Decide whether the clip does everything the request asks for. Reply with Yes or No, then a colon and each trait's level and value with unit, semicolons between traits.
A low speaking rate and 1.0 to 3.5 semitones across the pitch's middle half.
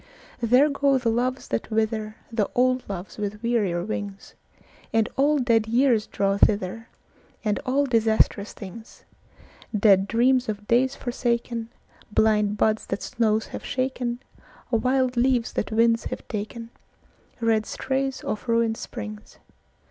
Yes: slow, 110 wpm; average, 2.8 semitones